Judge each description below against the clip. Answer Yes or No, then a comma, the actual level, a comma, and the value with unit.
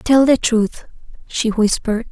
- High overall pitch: Yes, high, 230 Hz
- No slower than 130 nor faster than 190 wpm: Yes, average, 140 wpm